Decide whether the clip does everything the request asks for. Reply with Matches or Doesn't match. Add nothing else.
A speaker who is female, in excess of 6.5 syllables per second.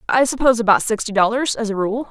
Matches